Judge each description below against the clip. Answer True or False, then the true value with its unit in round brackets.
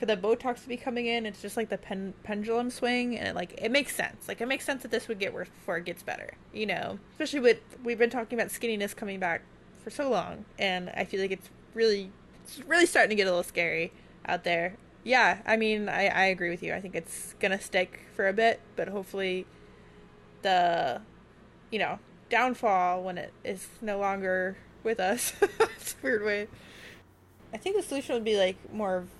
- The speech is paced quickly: True (215 wpm)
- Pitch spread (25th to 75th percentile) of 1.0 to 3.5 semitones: False (4.1 semitones)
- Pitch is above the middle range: True (210 Hz)